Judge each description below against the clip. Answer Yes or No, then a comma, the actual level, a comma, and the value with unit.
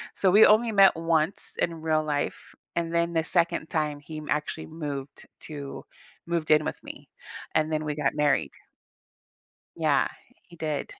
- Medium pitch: Yes, medium, 155 Hz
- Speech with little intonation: Yes, narrow, 2.0 semitones